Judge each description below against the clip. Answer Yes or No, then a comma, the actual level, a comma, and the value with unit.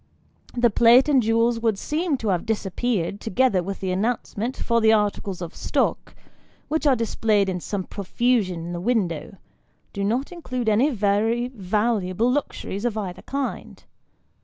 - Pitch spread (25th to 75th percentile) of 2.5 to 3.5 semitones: No, average, 3.9 semitones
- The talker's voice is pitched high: Yes, high, 220 Hz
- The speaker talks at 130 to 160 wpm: Yes, average, 155 wpm